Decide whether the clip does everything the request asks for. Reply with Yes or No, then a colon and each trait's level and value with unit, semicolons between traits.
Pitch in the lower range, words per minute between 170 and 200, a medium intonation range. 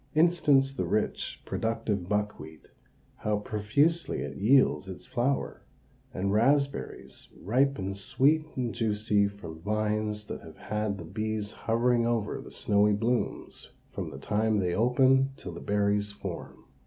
No: low, 105 Hz; slow, 135 wpm; average, 3.5 semitones